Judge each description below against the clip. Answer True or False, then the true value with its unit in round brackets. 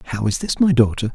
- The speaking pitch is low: True (125 Hz)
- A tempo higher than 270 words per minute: False (260 wpm)